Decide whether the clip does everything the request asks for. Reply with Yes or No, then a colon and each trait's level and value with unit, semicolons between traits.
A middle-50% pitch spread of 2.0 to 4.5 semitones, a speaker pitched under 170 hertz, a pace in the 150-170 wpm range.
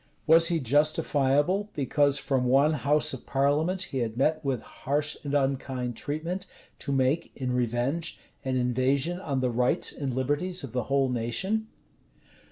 Yes: average, 3.3 semitones; medium, 140 Hz; average, 155 wpm